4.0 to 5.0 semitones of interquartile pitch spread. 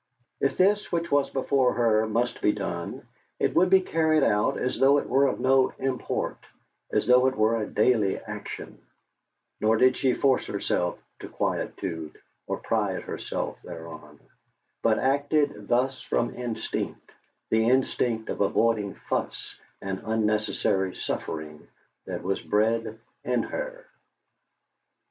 Yes: average, 4.4 semitones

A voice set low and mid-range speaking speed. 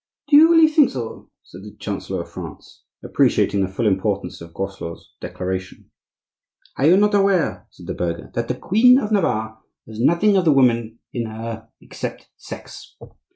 Yes: low, 120 Hz; average, 170 wpm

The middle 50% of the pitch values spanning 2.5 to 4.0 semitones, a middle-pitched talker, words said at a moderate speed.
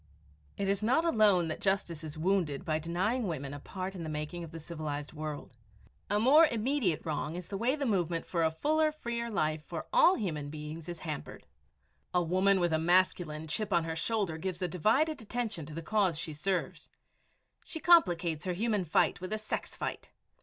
No: average, 5.2 semitones; medium, 175 Hz; average, 195 wpm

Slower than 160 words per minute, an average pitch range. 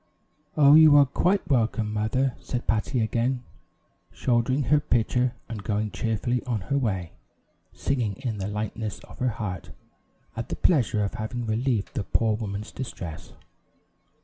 Yes: average, 150 wpm; average, 3.3 semitones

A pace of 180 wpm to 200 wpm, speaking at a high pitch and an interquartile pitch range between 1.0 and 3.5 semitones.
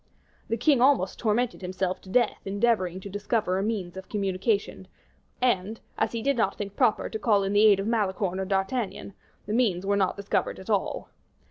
Yes: average, 195 wpm; high, 200 Hz; average, 3.0 semitones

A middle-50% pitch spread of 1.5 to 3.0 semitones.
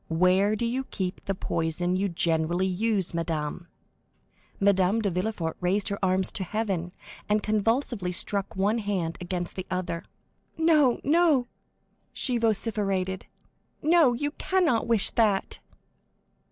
No: average, 4.1 semitones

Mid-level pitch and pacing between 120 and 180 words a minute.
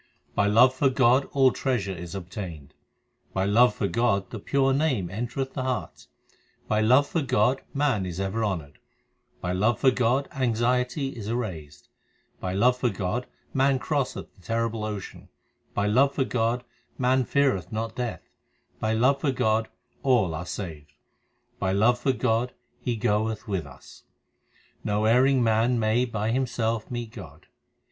No: low, 115 Hz; average, 155 wpm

